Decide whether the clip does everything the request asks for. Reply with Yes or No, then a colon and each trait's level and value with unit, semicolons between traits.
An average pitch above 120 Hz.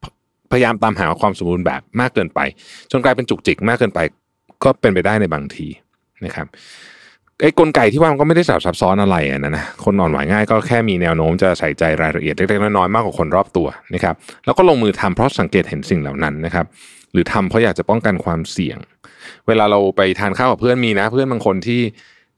No: low, 100 Hz